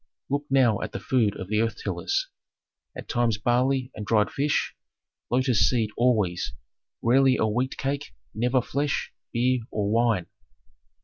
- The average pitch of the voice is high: No, low, 120 Hz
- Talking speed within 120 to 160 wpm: Yes, average, 145 wpm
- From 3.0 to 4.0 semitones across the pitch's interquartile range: Yes, average, 3.5 semitones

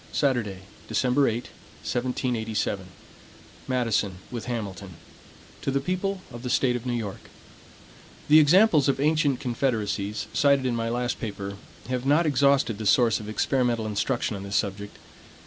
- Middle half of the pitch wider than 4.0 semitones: Yes, average, 4.4 semitones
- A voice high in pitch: No, low, 120 Hz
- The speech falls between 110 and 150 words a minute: Yes, average, 145 wpm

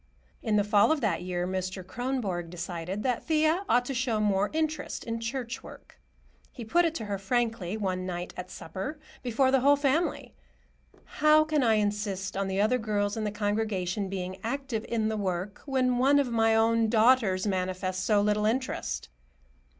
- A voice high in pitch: Yes, high, 215 Hz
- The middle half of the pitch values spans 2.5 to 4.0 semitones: No, average, 4.8 semitones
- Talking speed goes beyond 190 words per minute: No, average, 180 wpm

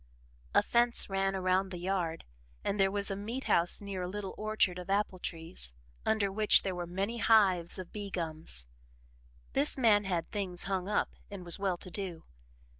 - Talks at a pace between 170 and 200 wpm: Yes, average, 180 wpm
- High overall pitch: Yes, high, 195 Hz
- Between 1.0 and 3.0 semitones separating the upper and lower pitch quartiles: Yes, narrow, 2.5 semitones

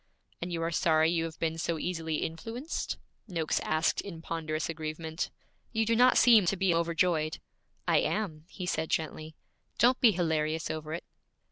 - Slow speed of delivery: No, average, 165 wpm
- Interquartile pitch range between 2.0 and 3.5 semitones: Yes, narrow, 2.4 semitones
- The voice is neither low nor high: Yes, medium, 165 Hz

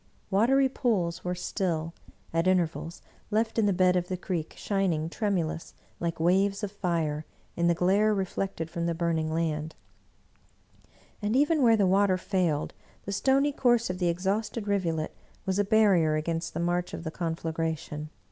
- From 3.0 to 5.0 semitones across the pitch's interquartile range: Yes, average, 3.6 semitones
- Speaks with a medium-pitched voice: Yes, medium, 180 Hz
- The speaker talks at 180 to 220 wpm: No, average, 165 wpm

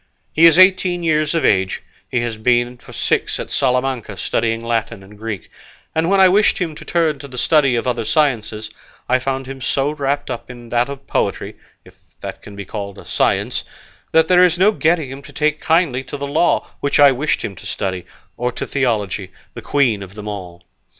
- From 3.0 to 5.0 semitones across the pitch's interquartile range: No, wide, 5.4 semitones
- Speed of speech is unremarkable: No, fast, 210 wpm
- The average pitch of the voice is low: Yes, low, 130 Hz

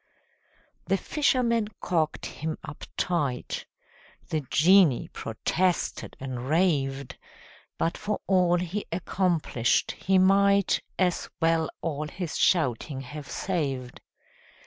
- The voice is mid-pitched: Yes, medium, 165 Hz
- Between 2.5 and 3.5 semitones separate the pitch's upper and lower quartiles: No, average, 4.9 semitones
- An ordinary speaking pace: No, slow, 100 wpm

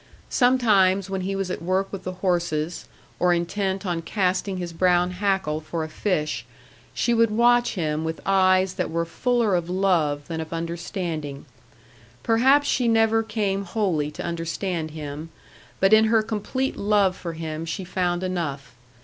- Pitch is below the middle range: No, medium, 185 Hz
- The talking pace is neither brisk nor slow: Yes, average, 160 wpm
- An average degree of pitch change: Yes, average, 3.6 semitones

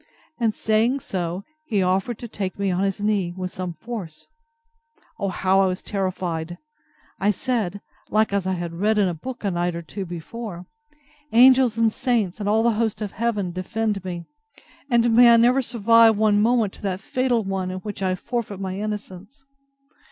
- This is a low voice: No, high, 205 Hz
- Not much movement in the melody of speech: No, average, 3.7 semitones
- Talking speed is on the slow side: No, average, 185 wpm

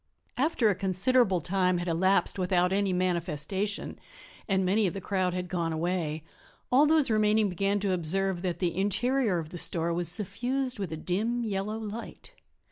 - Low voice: No, high, 190 Hz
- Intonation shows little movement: No, average, 3.2 semitones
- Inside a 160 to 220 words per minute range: Yes, average, 170 wpm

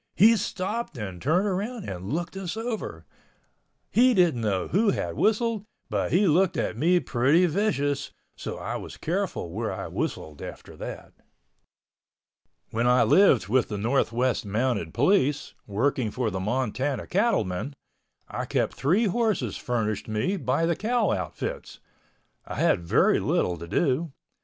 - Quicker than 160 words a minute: No, average, 145 wpm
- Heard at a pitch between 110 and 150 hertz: Yes, medium, 140 Hz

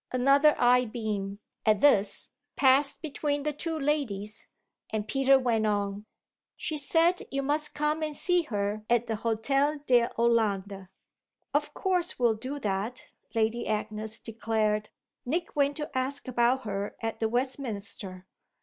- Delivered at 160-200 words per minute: No, average, 140 wpm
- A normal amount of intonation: Yes, average, 5.0 semitones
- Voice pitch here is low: No, high, 240 Hz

